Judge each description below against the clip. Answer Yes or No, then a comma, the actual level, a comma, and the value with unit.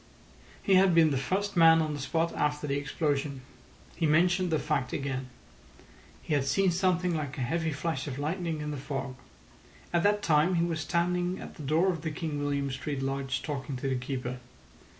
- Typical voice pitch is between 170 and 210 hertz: No, medium, 150 Hz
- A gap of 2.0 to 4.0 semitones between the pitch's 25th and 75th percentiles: Yes, average, 3.6 semitones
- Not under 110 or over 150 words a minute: No, average, 195 wpm